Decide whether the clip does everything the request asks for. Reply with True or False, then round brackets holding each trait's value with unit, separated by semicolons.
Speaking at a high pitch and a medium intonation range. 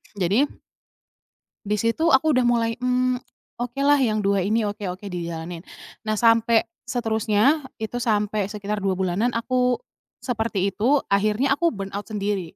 True (220 Hz; 3.7 semitones)